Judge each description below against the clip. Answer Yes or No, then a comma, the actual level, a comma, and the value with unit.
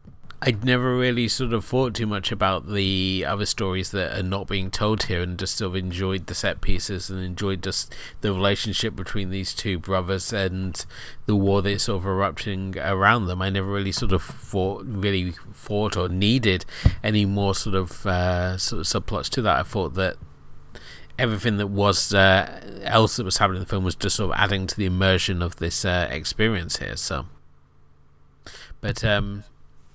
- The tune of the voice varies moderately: No, narrow, 2.1 semitones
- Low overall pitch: Yes, very low, 95 Hz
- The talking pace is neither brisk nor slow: Yes, average, 190 wpm